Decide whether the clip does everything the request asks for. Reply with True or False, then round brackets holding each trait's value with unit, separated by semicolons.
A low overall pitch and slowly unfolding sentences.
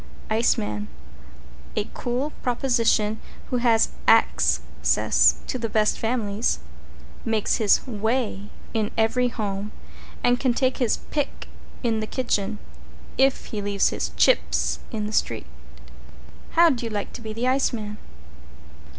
False (225 Hz; 130 wpm)